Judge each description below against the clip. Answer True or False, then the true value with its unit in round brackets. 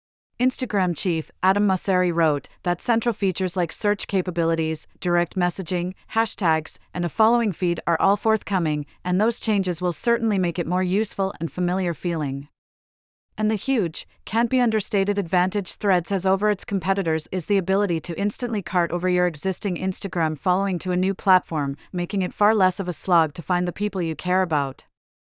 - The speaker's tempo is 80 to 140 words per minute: False (175 wpm)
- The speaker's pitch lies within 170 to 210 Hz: True (185 Hz)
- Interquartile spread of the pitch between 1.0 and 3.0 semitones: True (2.7 semitones)